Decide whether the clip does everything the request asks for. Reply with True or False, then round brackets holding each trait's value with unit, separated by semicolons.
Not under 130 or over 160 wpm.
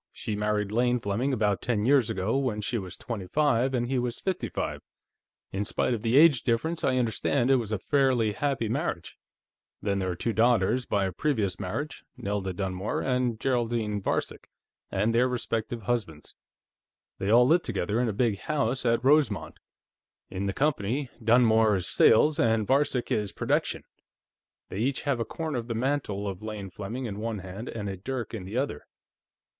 False (180 wpm)